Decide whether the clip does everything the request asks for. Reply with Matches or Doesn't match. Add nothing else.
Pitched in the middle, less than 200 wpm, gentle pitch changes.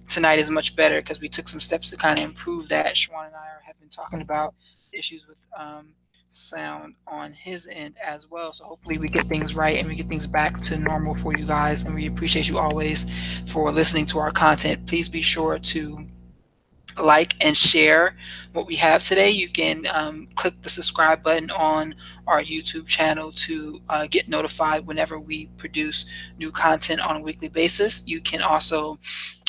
Matches